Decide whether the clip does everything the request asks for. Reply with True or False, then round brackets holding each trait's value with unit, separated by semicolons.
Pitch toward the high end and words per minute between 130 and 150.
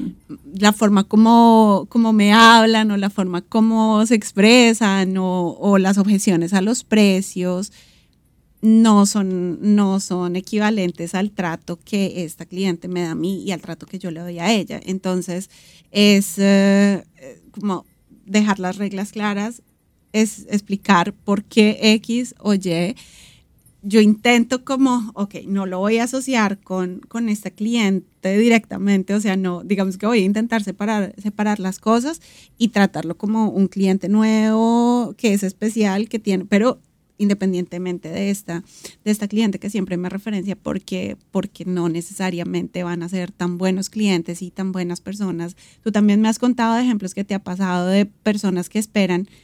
False (200 Hz; 165 wpm)